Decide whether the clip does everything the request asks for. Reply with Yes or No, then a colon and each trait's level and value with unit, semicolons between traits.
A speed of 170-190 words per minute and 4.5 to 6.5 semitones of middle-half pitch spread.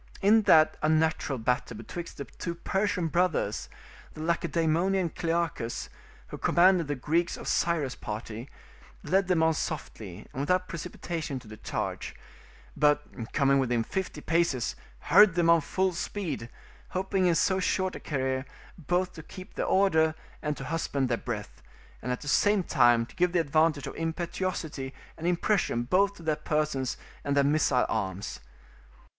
No: average, 155 wpm; average, 5.0 semitones